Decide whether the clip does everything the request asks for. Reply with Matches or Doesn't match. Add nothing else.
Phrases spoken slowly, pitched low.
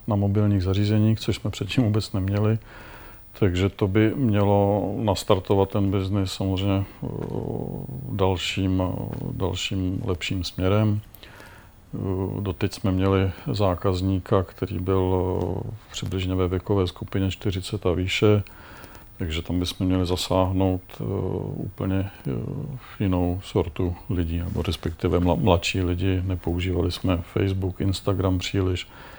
Matches